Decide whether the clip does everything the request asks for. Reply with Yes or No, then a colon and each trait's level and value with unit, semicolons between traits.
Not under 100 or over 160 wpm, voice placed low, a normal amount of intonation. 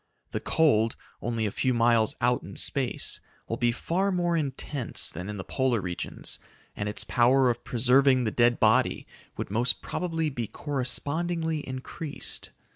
Yes: average, 155 wpm; low, 125 Hz; average, 4.0 semitones